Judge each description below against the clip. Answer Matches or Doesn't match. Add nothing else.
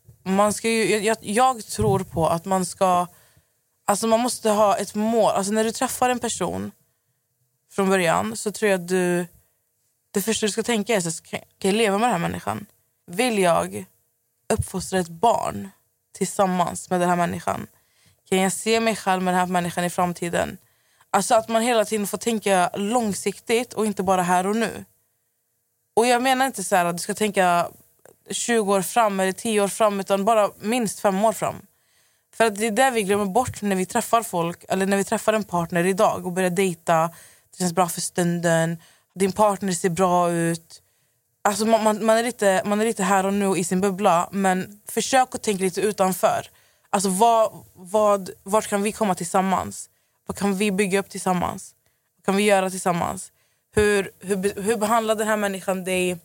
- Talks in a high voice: Matches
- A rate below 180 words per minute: Doesn't match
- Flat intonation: Doesn't match